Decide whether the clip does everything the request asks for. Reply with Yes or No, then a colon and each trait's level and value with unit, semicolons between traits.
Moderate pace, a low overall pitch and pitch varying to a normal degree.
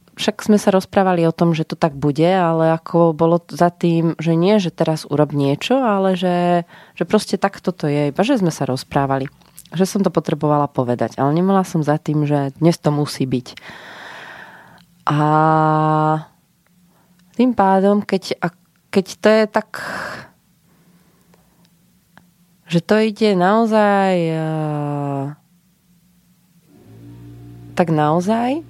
No: average, 130 wpm; medium, 170 Hz; average, 3.3 semitones